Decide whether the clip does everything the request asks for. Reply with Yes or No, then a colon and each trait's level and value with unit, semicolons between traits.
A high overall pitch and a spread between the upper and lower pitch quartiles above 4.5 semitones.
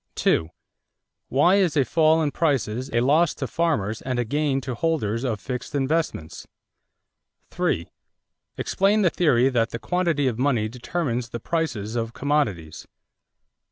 No: low, 135 Hz; wide, 5.6 semitones